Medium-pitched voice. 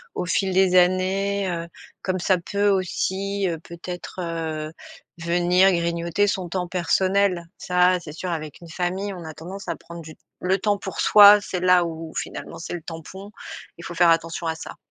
Yes: medium, 180 Hz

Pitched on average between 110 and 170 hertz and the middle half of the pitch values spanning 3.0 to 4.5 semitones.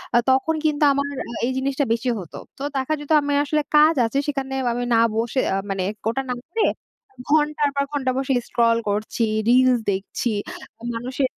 No: very high, 265 Hz; average, 3.5 semitones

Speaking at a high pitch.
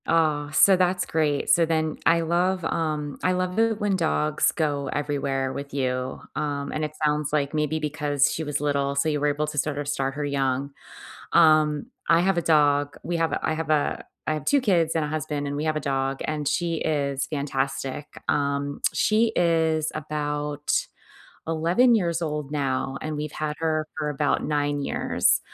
No: medium, 150 Hz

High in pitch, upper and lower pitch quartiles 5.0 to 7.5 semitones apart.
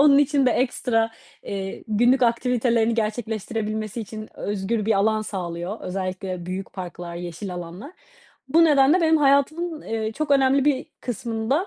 Yes: high, 225 Hz; wide, 5.6 semitones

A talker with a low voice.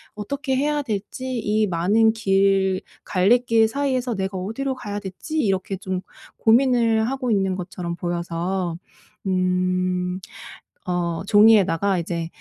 No: high, 195 Hz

